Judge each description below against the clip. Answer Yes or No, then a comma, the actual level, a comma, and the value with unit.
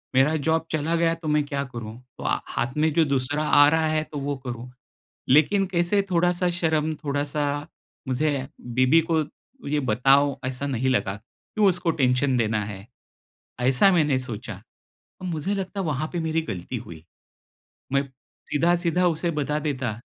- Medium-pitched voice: Yes, medium, 145 Hz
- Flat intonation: No, average, 4.1 semitones